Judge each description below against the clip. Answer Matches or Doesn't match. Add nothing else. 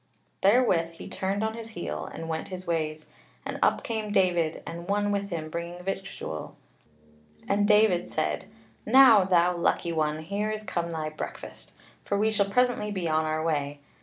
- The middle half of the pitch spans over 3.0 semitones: Matches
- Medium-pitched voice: Matches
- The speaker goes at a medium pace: Matches